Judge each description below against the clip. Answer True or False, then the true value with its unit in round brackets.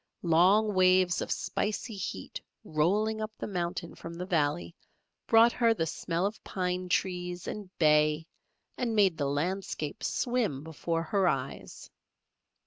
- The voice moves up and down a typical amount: True (4.1 semitones)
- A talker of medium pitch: True (180 Hz)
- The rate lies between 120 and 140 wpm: True (135 wpm)